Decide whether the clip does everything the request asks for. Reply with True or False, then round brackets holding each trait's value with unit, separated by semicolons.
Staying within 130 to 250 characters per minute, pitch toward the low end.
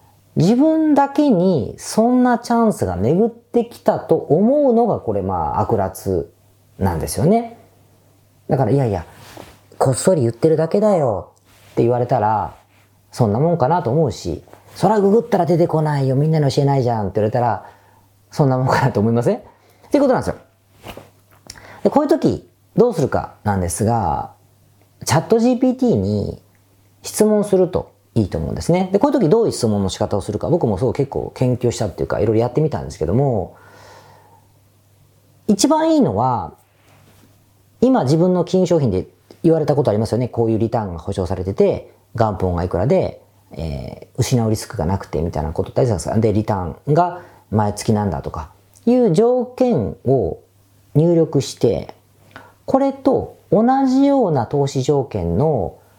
False (340 characters per minute; 120 Hz)